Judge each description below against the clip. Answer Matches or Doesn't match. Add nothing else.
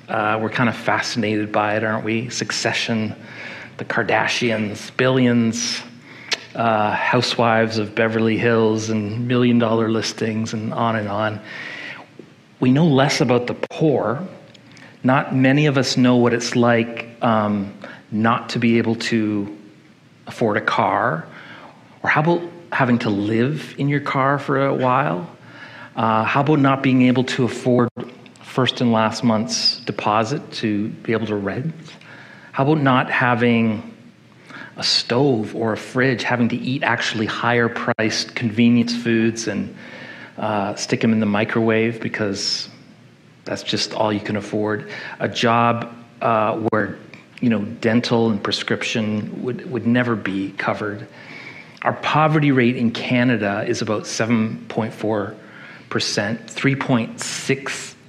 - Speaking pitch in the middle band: Doesn't match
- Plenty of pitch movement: Doesn't match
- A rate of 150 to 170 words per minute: Doesn't match